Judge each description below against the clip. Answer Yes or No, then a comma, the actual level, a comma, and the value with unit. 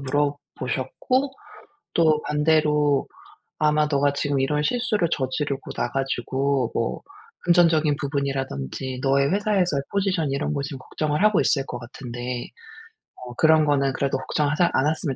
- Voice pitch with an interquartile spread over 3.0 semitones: No, narrow, 2.6 semitones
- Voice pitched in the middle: Yes, medium, 145 Hz